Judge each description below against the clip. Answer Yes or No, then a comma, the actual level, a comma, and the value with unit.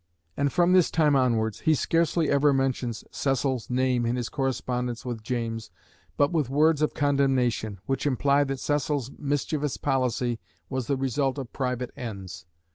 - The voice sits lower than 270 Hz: Yes, low, 135 Hz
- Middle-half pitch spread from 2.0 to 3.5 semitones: Yes, average, 2.8 semitones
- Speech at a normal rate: Yes, average, 155 wpm